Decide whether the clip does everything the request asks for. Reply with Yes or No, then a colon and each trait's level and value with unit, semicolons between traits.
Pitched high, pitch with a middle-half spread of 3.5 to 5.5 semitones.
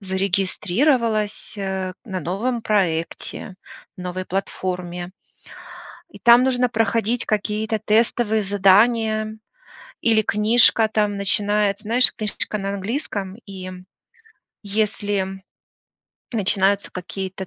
No: high, 205 Hz; narrow, 2.5 semitones